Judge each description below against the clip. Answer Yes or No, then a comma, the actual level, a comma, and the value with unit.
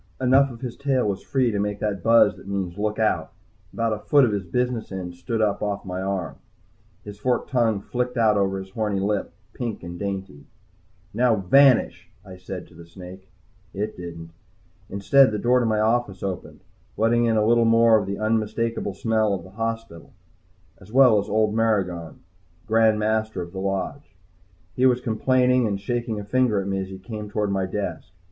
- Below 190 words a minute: No, average, 195 wpm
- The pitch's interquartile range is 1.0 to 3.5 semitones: Yes, average, 3.2 semitones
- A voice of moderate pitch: No, low, 105 Hz